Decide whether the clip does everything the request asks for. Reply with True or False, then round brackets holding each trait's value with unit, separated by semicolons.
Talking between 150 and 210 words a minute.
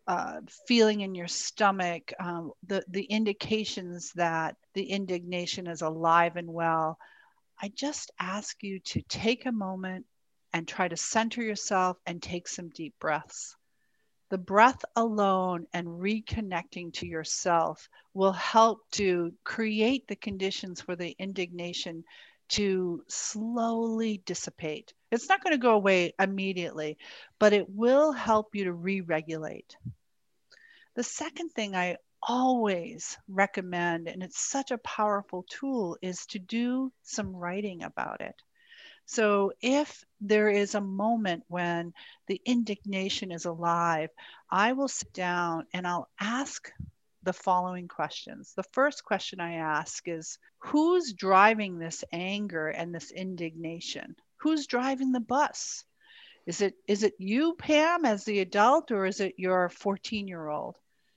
False (140 wpm)